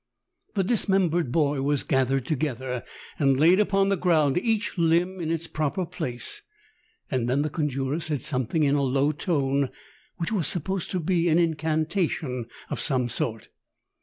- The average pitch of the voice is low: No, medium, 155 Hz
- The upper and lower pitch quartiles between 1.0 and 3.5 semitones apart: No, average, 4.4 semitones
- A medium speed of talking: Yes, average, 170 wpm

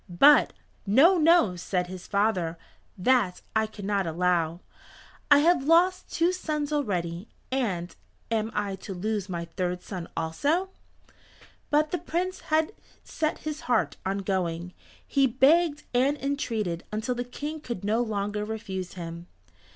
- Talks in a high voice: Yes, high, 220 Hz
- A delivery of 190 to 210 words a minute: No, average, 140 wpm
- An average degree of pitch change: No, wide, 8.4 semitones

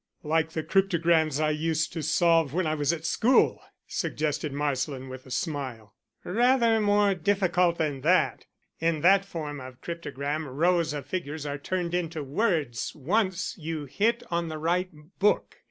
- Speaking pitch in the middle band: Yes, medium, 160 Hz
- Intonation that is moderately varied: Yes, average, 3.6 semitones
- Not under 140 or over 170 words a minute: Yes, average, 155 wpm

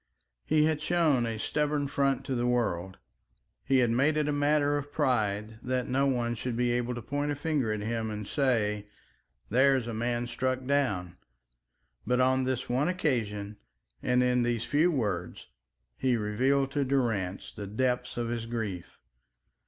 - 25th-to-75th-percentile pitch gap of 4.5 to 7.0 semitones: No, average, 3.6 semitones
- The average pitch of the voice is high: No, low, 125 Hz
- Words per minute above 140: Yes, average, 170 wpm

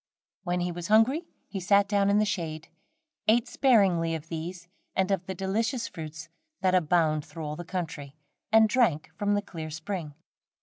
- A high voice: No, medium, 180 Hz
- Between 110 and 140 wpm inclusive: No, average, 175 wpm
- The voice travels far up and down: No, average, 4.0 semitones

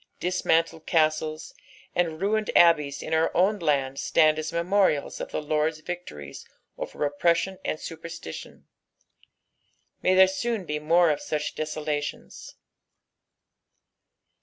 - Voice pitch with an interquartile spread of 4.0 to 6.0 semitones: No, average, 2.8 semitones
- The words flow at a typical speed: No, slow, 115 wpm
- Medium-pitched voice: Yes, medium, 160 Hz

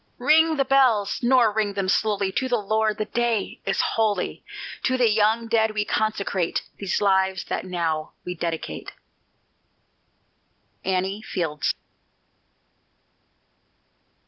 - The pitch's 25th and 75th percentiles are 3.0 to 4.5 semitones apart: Yes, average, 3.4 semitones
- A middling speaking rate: No, slow, 120 wpm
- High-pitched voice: Yes, high, 210 Hz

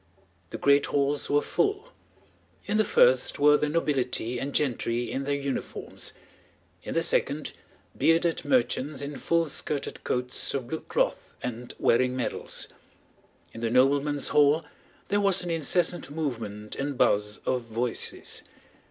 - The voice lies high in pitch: No, medium, 140 Hz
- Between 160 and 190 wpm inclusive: No, average, 140 wpm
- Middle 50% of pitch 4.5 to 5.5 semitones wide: No, average, 4.0 semitones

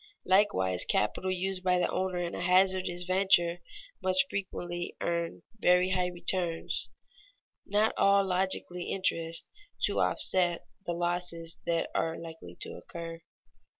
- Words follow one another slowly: Yes, slow, 125 wpm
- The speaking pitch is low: No, medium, 180 Hz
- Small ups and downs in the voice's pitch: Yes, narrow, 1.7 semitones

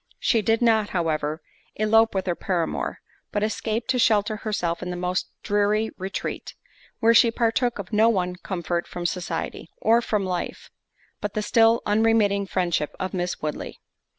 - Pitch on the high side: Yes, high, 205 Hz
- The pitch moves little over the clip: No, average, 3.8 semitones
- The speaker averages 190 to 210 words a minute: No, average, 160 wpm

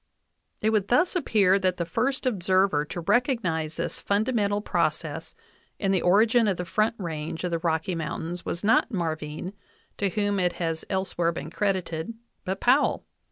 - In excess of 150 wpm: Yes, average, 160 wpm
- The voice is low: No, high, 190 Hz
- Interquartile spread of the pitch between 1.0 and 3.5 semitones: No, average, 4.1 semitones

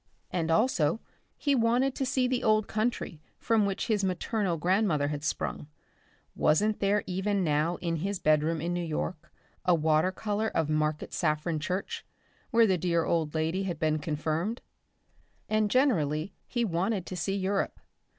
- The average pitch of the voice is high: No, medium, 180 Hz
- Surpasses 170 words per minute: No, average, 160 wpm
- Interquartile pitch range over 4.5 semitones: Yes, average, 5.2 semitones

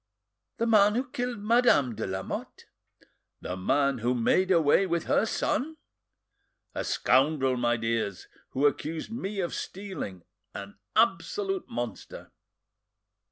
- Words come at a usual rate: No, slow, 120 wpm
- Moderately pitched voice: Yes, medium, 160 Hz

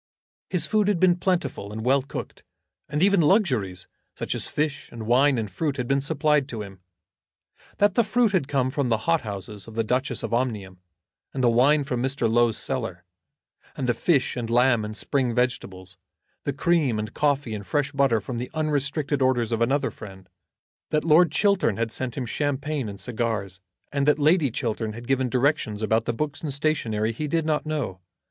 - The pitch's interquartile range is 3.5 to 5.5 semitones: Yes, average, 4.9 semitones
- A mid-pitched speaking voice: No, low, 130 Hz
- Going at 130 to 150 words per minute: No, average, 195 wpm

